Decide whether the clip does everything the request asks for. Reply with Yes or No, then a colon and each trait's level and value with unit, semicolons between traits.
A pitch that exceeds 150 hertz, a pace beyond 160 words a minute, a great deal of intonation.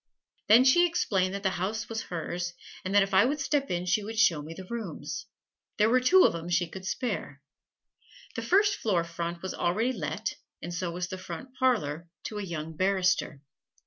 No: high, 190 Hz; average, 200 wpm; average, 4.9 semitones